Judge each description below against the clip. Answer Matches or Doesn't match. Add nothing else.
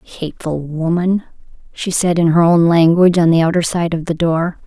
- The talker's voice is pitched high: Doesn't match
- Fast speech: Doesn't match